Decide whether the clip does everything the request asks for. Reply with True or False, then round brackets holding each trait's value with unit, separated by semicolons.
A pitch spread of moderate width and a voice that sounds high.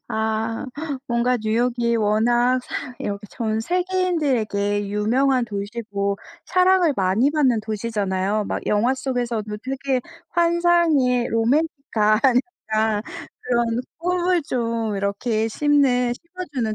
True (4.4 semitones; 235 Hz)